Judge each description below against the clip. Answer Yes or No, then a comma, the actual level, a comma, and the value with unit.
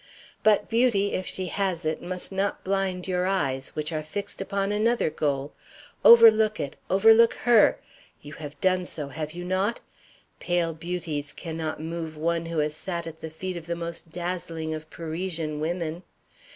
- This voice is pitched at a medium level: Yes, medium, 170 Hz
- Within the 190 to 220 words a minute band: No, average, 165 wpm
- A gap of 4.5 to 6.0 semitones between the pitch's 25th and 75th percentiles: No, average, 3.5 semitones